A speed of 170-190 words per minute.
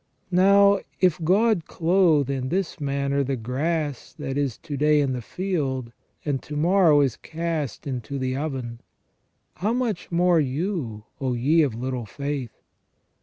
No: average, 150 wpm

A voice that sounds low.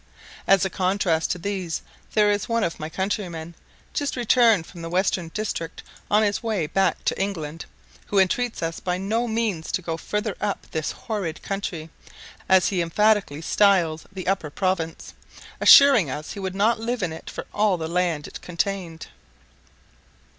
No: high, 190 Hz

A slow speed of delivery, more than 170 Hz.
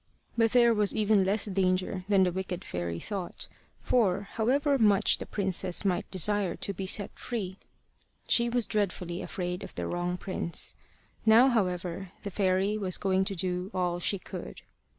No: average, 165 wpm; high, 190 Hz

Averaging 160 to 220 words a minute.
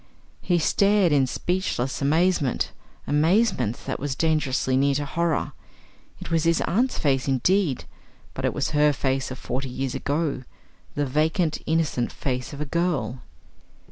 No: average, 145 wpm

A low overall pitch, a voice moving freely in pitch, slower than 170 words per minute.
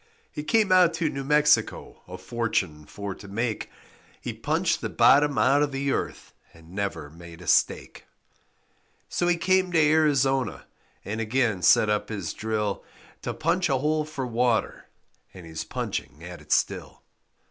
Yes: low, 125 Hz; wide, 7.4 semitones; average, 160 wpm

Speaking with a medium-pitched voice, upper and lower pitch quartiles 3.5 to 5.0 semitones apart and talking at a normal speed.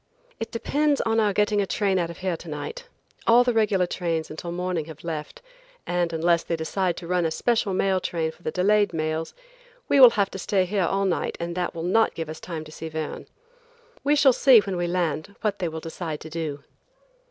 No: medium, 180 Hz; average, 4.0 semitones; fast, 220 wpm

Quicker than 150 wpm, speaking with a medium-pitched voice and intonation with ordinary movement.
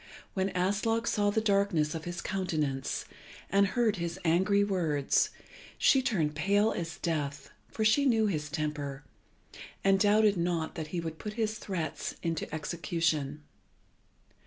No: average, 140 wpm; medium, 175 Hz; average, 4.6 semitones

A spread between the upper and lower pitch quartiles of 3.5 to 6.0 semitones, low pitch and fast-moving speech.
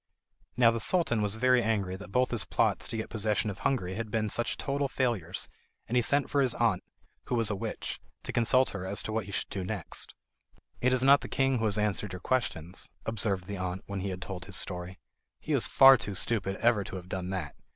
Yes: average, 4.0 semitones; low, 105 Hz; fast, 235 wpm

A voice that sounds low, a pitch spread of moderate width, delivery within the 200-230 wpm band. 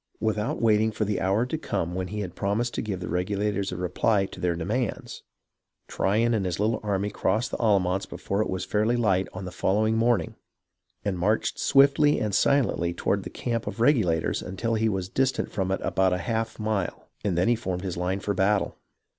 Yes: low, 105 Hz; average, 3.2 semitones; fast, 205 wpm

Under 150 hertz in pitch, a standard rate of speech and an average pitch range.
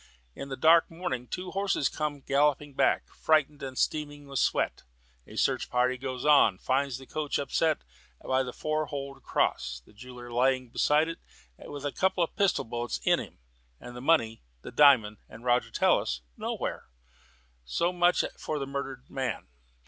Yes: medium, 140 Hz; average, 170 wpm; average, 3.4 semitones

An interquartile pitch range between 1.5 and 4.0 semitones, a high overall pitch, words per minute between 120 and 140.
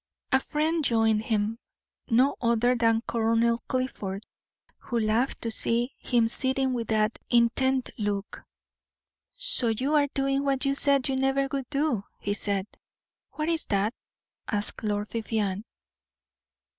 Yes: average, 3.7 semitones; high, 235 Hz; slow, 135 wpm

